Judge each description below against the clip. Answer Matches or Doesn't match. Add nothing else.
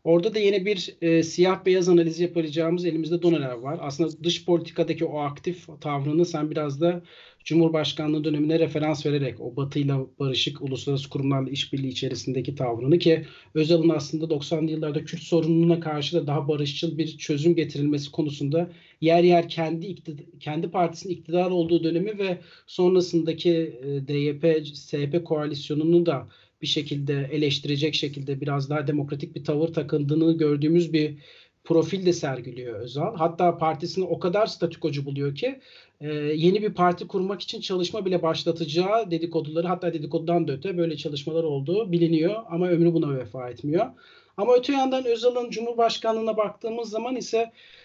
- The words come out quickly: Matches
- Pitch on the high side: Doesn't match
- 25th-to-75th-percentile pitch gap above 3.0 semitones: Doesn't match